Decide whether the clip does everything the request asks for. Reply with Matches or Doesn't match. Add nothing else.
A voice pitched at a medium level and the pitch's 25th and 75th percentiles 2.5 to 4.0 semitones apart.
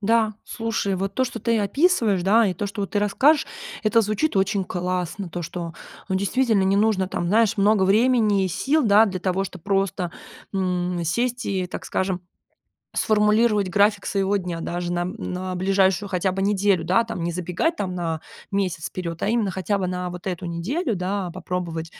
Doesn't match